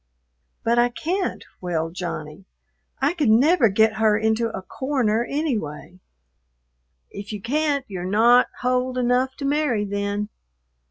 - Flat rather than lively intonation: No, average, 4.7 semitones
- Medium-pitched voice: No, high, 225 Hz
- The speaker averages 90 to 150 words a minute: Yes, average, 140 wpm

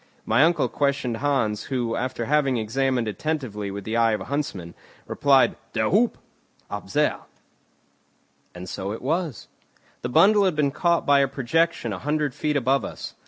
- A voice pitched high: No, low, 135 Hz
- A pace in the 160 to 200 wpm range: Yes, average, 165 wpm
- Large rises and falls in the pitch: No, average, 4.9 semitones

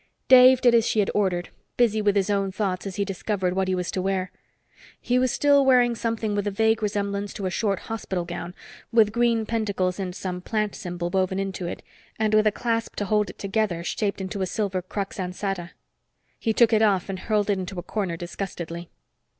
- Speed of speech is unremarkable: No, fast, 210 wpm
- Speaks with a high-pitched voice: Yes, high, 200 Hz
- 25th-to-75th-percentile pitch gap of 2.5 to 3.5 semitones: Yes, average, 2.8 semitones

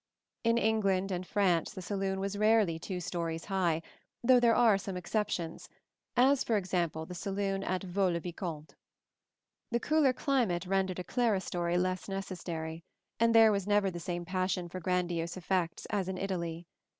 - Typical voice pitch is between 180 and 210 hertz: Yes, medium, 185 Hz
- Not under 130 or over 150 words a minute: No, average, 160 wpm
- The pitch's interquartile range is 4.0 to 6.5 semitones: No, average, 2.9 semitones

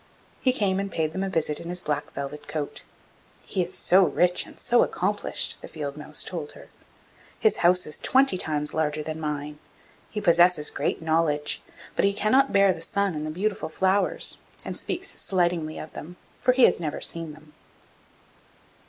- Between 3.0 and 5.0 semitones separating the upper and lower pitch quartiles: Yes, average, 4.1 semitones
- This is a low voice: No, medium, 170 Hz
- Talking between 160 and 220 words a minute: Yes, average, 180 wpm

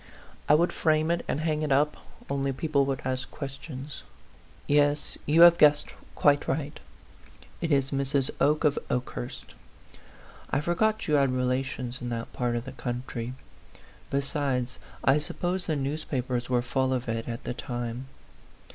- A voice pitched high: No, low, 135 Hz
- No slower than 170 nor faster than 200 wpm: No, average, 155 wpm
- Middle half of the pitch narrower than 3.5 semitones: Yes, average, 2.9 semitones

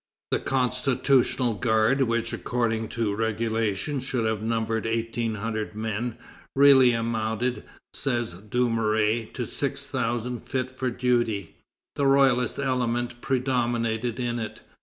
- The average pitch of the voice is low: Yes, low, 115 Hz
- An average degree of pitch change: No, narrow, 2.1 semitones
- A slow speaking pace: Yes, slow, 115 wpm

